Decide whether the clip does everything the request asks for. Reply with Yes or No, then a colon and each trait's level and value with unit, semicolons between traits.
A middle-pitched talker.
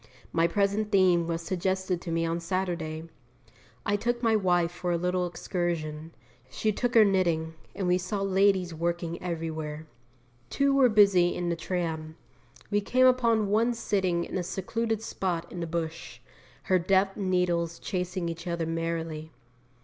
Yes: medium, 180 Hz